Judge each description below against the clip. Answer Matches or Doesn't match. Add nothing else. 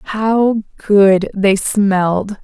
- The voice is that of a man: Doesn't match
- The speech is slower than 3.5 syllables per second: Matches